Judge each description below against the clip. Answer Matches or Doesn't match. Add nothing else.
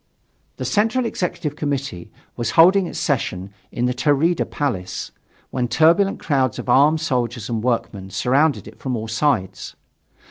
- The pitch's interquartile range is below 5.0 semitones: Doesn't match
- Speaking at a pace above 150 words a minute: Doesn't match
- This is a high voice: Doesn't match